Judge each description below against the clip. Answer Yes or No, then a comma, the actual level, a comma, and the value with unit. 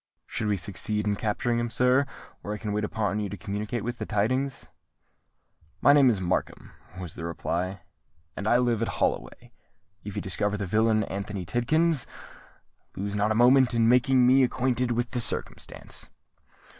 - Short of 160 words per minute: No, average, 170 wpm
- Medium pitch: No, low, 110 Hz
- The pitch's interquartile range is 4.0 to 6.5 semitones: No, average, 3.3 semitones